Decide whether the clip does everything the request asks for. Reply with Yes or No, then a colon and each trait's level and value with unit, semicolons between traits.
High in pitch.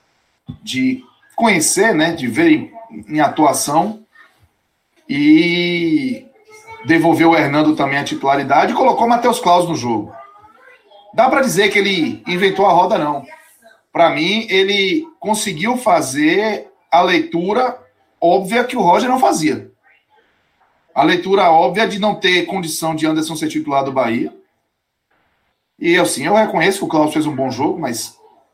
Yes: high, 205 Hz